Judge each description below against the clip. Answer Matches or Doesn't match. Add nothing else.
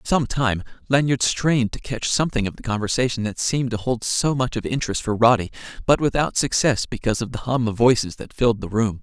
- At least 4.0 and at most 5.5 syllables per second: Doesn't match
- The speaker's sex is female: Doesn't match